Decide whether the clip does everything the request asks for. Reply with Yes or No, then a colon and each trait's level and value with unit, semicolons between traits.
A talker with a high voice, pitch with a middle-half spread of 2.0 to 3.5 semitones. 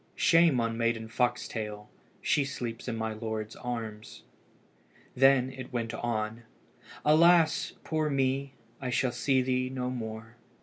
No: low, 125 Hz; average, 2.9 semitones